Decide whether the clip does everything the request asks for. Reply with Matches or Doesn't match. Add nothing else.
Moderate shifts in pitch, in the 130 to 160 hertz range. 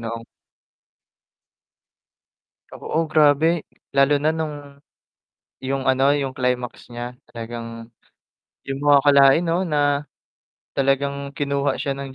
Doesn't match